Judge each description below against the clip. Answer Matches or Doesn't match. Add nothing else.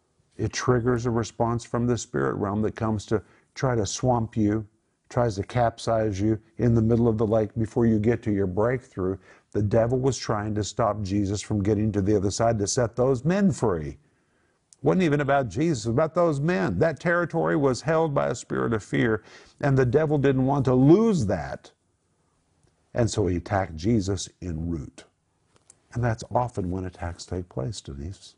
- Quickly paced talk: Doesn't match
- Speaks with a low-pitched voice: Matches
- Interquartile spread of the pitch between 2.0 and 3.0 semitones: Doesn't match